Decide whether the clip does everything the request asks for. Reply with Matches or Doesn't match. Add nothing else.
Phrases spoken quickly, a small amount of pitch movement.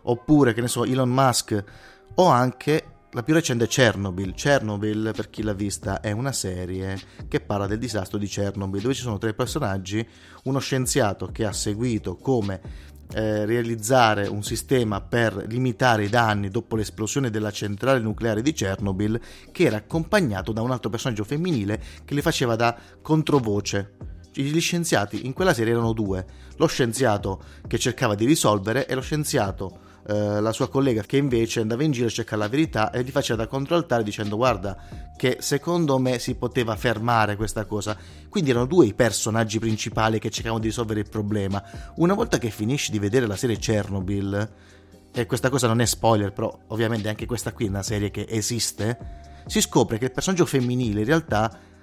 Doesn't match